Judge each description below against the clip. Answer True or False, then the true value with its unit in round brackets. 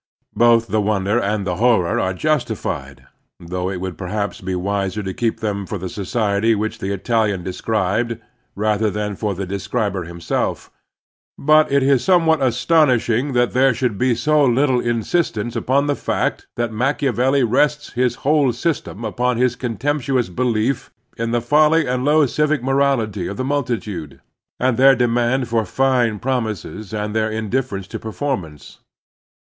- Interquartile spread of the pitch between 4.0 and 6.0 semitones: True (4.5 semitones)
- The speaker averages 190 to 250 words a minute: False (160 wpm)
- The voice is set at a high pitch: False (115 Hz)